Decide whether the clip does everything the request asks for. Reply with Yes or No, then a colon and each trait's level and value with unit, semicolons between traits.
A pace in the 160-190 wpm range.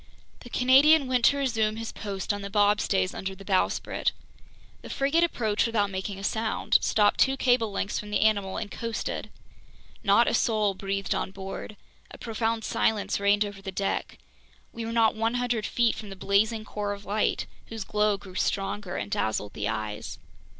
Yes: average, 180 wpm